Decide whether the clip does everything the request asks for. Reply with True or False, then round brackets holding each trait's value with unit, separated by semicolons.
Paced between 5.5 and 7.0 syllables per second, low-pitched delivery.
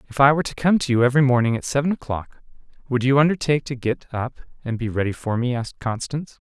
True (6.9 syllables/s; 130 Hz)